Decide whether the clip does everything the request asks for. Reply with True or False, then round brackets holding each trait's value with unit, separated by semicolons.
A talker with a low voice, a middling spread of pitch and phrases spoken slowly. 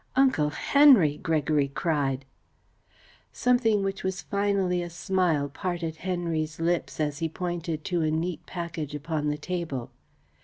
False (165 Hz; 3.3 semitones; 130 wpm)